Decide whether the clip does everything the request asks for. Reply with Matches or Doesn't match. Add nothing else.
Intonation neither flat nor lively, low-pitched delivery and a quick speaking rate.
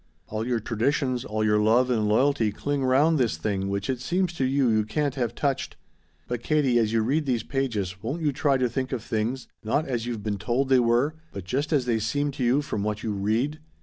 Matches